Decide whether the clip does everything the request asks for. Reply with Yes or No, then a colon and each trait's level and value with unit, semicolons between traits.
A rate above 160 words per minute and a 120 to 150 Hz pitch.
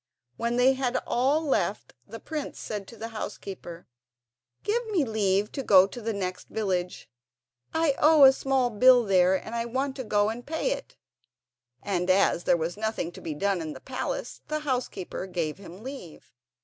No: average, 175 wpm; high, 220 Hz